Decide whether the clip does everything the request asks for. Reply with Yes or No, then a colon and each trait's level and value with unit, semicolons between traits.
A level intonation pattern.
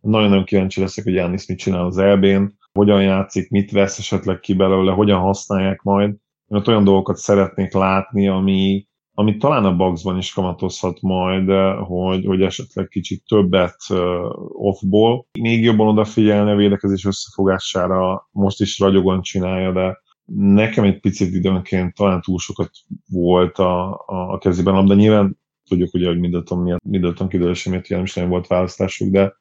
Yes: narrow, 1.4 semitones